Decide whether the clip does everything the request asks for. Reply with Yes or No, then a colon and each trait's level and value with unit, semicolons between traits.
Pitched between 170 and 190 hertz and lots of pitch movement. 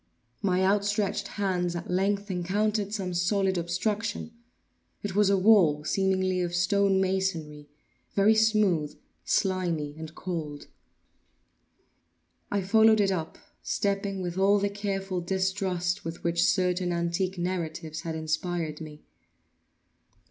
No: medium, 185 Hz; average, 2.7 semitones